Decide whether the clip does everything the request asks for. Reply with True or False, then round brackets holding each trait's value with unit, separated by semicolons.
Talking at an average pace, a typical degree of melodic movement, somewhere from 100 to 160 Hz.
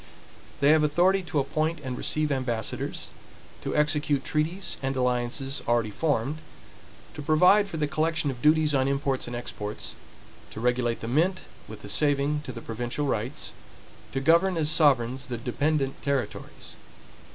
True (150 wpm; 3.9 semitones; 140 Hz)